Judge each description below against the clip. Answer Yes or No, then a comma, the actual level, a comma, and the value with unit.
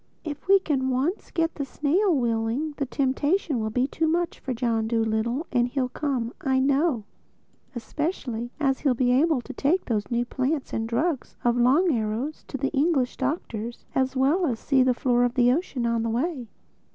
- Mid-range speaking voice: No, very high, 260 Hz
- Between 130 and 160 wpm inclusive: No, average, 185 wpm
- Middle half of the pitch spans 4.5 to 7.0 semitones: No, average, 4.0 semitones